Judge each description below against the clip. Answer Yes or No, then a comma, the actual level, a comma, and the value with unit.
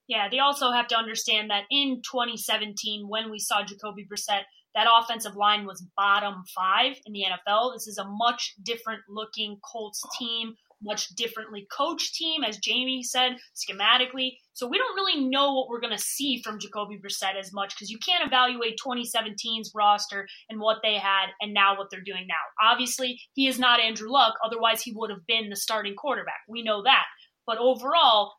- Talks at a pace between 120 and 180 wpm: No, average, 190 wpm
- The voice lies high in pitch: Yes, high, 225 Hz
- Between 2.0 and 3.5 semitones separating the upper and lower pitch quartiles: Yes, average, 3.1 semitones